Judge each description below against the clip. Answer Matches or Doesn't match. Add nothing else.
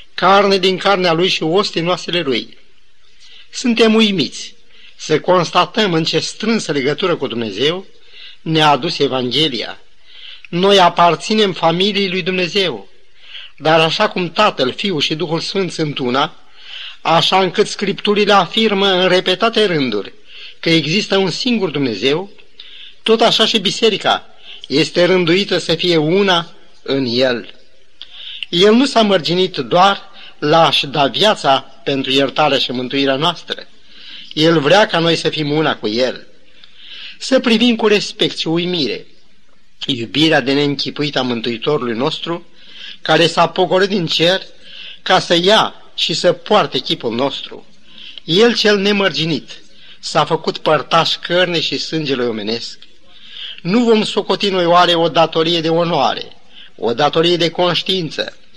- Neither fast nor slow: Matches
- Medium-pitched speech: Matches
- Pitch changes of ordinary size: Matches